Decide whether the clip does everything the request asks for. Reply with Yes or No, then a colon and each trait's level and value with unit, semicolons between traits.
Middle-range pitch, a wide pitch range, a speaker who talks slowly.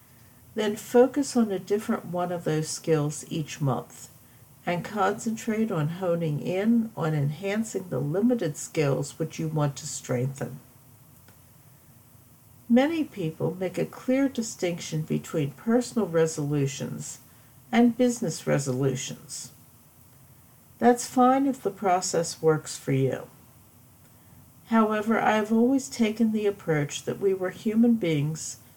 Yes: medium, 165 Hz; wide, 8.1 semitones; slow, 120 wpm